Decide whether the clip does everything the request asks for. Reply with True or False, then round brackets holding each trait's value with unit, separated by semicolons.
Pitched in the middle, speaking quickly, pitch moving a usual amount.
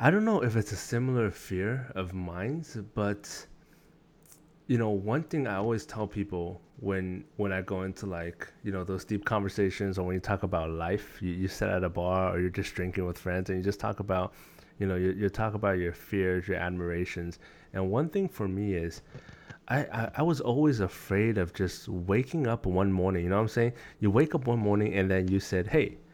False (100 Hz; 220 wpm; 3.6 semitones)